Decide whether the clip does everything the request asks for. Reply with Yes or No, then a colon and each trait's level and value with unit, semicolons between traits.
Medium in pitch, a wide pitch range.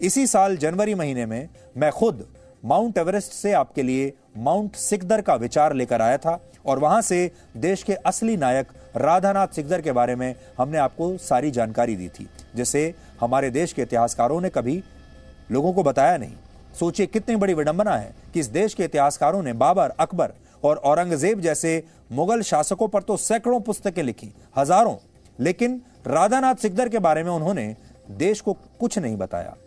Yes: medium, 165 Hz; wide, 7.8 semitones